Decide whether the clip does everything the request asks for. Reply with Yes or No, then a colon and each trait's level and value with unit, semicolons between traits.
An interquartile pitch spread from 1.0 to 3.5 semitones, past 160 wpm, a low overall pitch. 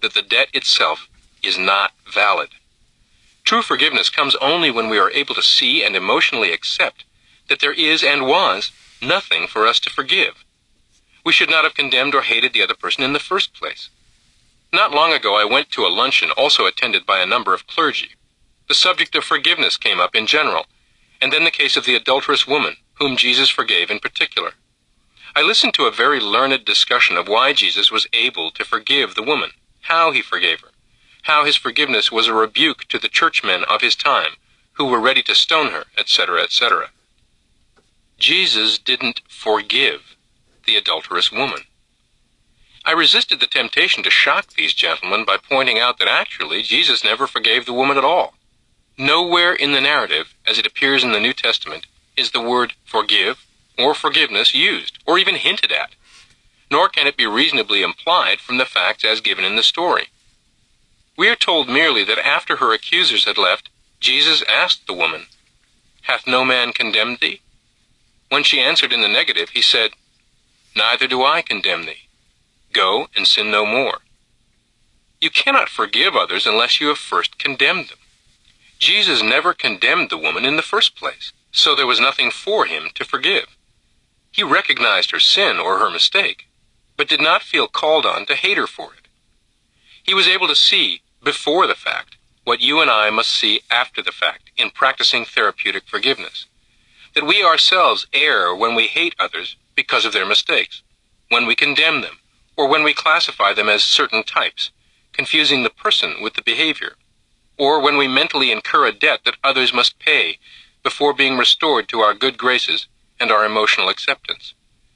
No: average, 4.0 semitones; average, 175 wpm; low, 125 Hz